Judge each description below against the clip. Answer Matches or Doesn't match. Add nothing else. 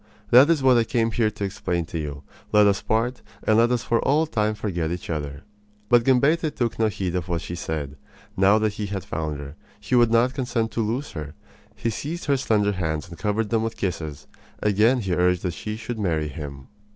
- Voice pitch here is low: Matches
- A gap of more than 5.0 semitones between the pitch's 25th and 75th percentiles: Matches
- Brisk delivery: Matches